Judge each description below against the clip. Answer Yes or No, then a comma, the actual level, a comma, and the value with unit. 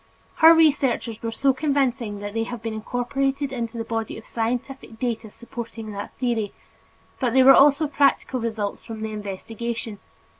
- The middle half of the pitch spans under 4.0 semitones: Yes, average, 3.3 semitones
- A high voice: Yes, high, 235 Hz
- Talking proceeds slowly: No, average, 160 wpm